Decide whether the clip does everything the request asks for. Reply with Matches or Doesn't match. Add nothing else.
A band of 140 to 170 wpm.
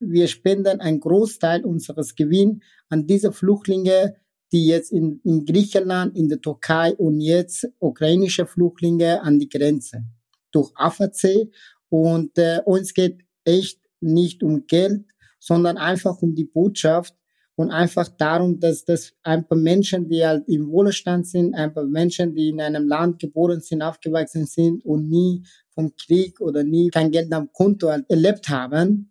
Matches